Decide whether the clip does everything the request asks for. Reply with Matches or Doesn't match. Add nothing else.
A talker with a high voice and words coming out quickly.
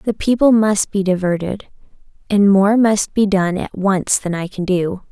Doesn't match